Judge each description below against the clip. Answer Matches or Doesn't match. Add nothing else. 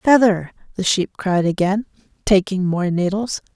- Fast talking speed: Doesn't match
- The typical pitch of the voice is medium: Doesn't match